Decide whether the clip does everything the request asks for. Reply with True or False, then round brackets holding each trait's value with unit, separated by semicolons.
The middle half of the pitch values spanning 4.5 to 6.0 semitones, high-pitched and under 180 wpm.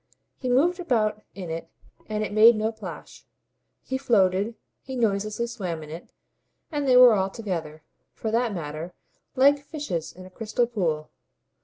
True (5.1 semitones; 215 Hz; 160 wpm)